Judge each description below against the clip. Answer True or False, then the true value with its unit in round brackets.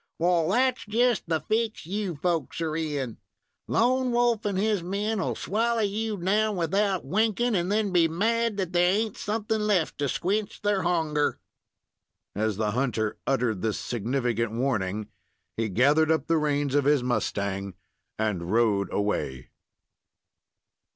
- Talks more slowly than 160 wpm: True (145 wpm)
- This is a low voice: False (170 Hz)